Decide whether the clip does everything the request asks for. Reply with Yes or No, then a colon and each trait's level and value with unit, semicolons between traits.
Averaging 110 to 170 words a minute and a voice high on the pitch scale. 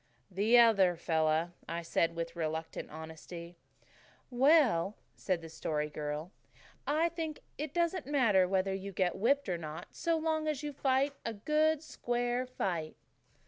Yes: average, 145 wpm; high, 200 Hz